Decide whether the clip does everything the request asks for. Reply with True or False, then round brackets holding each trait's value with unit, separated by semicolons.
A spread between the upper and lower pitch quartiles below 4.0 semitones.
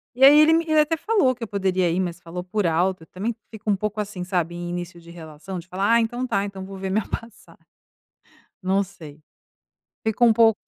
False (4.4 semitones)